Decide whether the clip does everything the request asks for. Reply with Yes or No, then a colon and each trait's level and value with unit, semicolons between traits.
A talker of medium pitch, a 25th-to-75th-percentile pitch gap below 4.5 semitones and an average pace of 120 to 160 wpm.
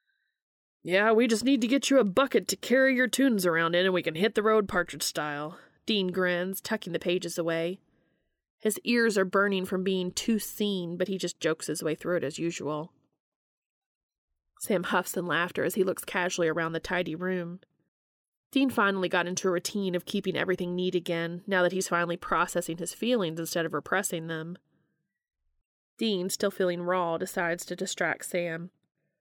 No: medium, 180 Hz; average, 2.8 semitones; average, 185 wpm